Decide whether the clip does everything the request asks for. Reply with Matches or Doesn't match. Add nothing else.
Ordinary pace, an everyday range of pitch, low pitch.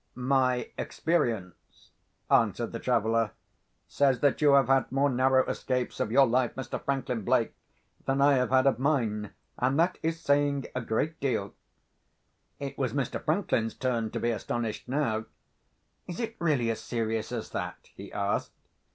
Matches